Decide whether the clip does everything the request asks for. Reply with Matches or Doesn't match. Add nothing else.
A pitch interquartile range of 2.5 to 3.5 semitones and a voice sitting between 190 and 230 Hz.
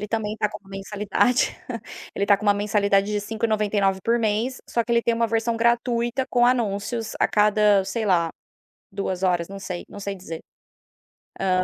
Matches